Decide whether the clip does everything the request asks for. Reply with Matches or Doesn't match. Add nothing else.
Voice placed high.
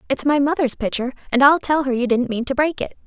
Matches